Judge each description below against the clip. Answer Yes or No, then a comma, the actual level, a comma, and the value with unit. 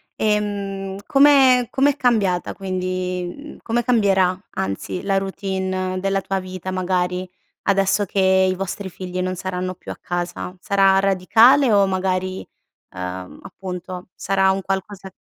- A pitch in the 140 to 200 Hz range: Yes, high, 190 Hz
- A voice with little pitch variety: Yes, narrow, 1.3 semitones